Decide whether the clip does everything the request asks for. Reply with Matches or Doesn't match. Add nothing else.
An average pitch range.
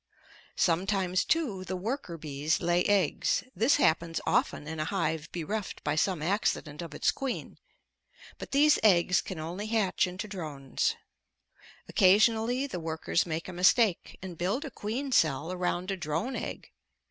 Matches